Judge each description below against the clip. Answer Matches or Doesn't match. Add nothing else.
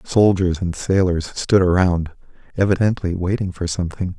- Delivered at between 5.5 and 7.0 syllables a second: Doesn't match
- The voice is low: Matches